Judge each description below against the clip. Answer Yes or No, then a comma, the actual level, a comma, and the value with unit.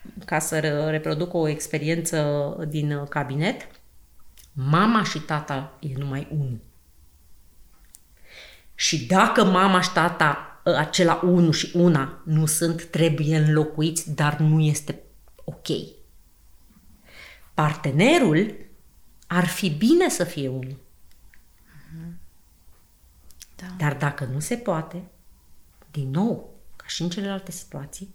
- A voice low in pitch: No, medium, 155 Hz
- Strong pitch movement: No, average, 4.8 semitones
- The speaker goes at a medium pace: No, slow, 105 wpm